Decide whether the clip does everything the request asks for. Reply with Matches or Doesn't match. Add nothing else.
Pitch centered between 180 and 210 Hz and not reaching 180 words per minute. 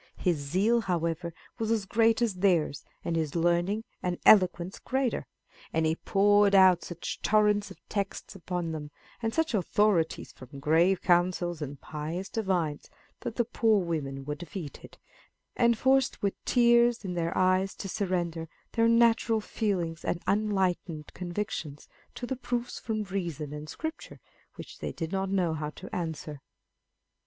Matches